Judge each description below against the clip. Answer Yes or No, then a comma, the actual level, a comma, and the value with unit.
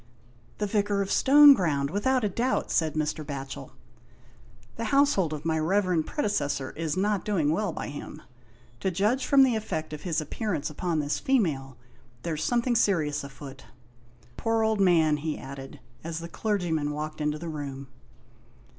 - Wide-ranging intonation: Yes, wide, 5.9 semitones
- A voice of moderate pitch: Yes, medium, 165 Hz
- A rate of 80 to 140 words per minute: No, average, 165 wpm